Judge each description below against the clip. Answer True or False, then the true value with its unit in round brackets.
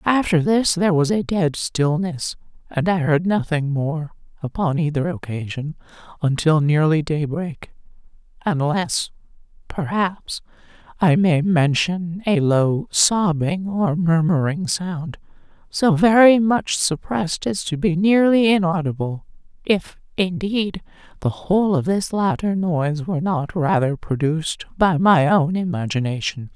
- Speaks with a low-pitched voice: False (170 Hz)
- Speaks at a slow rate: True (120 wpm)